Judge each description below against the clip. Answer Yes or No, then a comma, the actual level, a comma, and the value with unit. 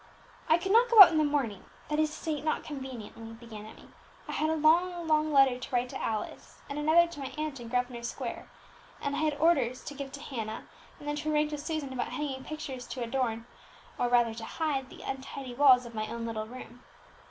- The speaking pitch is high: Yes, very high, 275 Hz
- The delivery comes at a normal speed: No, fast, 225 wpm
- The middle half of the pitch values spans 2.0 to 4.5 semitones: Yes, average, 4.2 semitones